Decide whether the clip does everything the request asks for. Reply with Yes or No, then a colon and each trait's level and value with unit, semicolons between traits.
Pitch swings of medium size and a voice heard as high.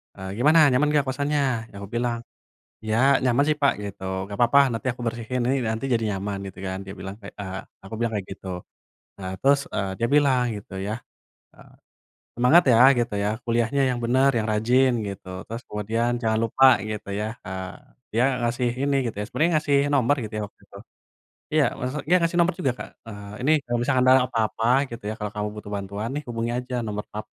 No: average, 4.0 semitones; low, 120 Hz